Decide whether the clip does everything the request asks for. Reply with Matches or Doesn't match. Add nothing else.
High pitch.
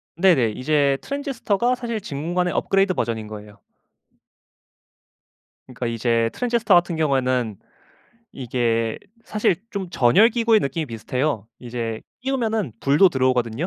Doesn't match